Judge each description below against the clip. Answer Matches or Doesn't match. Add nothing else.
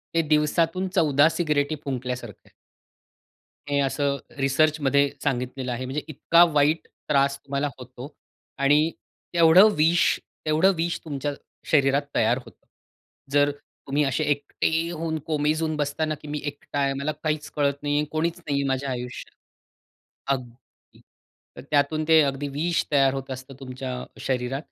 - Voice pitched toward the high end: Doesn't match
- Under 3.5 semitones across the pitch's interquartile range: Matches